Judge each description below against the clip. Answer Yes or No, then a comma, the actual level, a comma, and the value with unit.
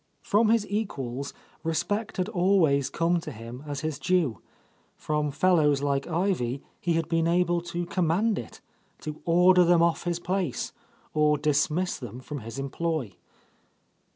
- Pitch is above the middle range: No, medium, 165 Hz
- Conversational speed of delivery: Yes, average, 155 wpm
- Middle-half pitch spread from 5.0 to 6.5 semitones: No, average, 4.1 semitones